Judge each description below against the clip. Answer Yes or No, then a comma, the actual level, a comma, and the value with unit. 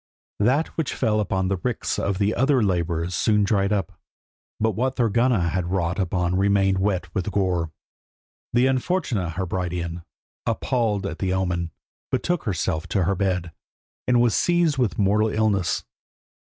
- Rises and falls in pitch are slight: No, average, 3.9 semitones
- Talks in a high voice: No, low, 100 Hz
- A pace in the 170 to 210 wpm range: No, average, 150 wpm